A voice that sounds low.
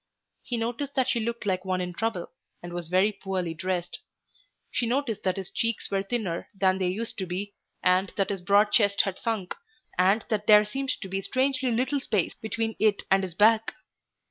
No: high, 205 Hz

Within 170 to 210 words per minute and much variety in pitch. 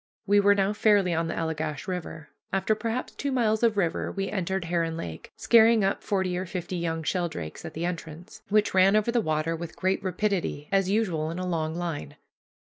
No: average, 200 wpm; average, 3.7 semitones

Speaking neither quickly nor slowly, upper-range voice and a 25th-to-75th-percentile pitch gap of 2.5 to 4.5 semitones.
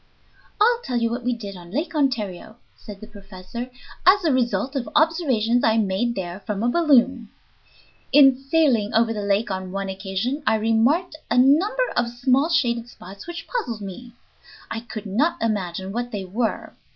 No: average, 175 wpm; high, 235 Hz; average, 5.0 semitones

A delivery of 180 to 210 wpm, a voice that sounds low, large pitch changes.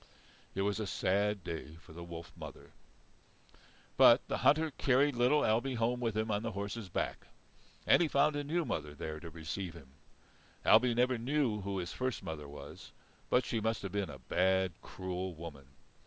Yes: average, 185 wpm; low, 100 Hz; wide, 6.5 semitones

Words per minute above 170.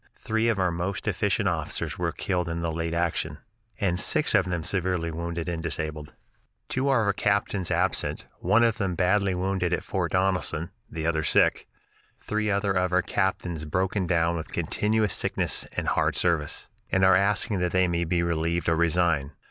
Yes: average, 180 wpm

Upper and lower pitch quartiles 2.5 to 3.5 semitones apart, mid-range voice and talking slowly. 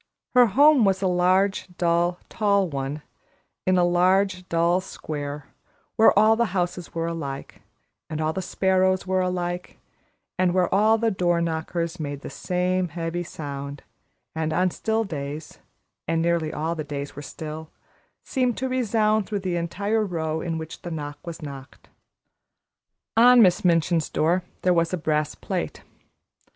No: average, 3.1 semitones; medium, 175 Hz; average, 155 wpm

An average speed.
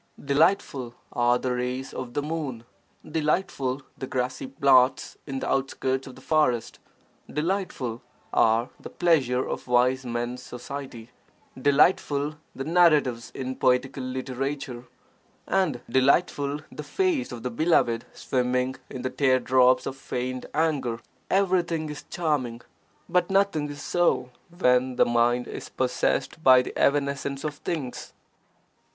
No: slow, 130 wpm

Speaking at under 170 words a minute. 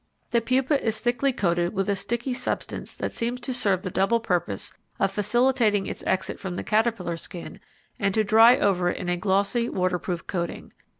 No: average, 185 wpm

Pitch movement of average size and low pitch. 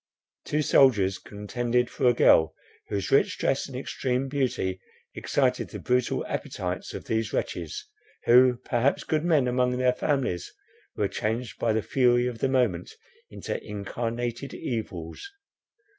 Yes: average, 3.1 semitones; low, 125 Hz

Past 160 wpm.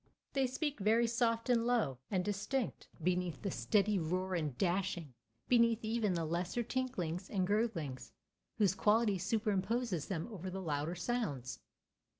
No: average, 145 wpm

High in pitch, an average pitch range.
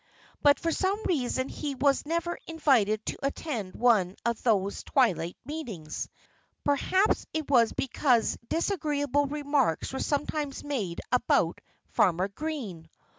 No: very high, 275 Hz; wide, 5.8 semitones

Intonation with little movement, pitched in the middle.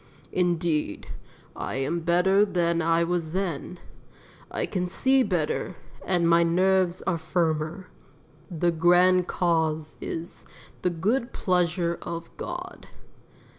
Yes: narrow, 1.8 semitones; medium, 175 Hz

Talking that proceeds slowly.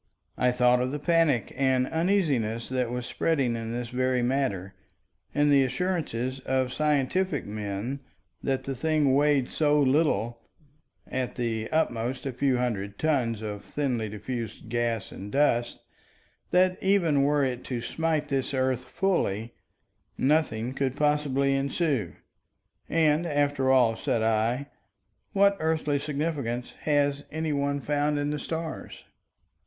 Yes: slow, 130 wpm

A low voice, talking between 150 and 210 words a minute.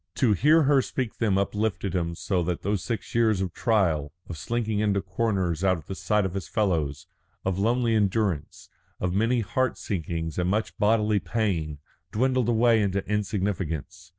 Yes: low, 100 Hz; average, 170 wpm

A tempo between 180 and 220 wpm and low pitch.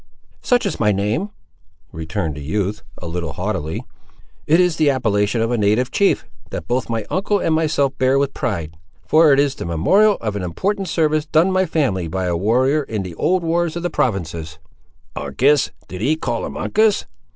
Yes: average, 190 wpm; low, 125 Hz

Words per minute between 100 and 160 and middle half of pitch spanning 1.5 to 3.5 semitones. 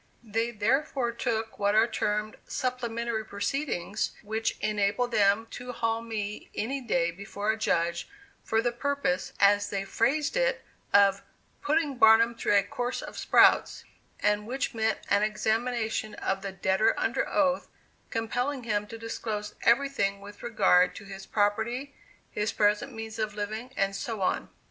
Yes: average, 150 wpm; average, 2.8 semitones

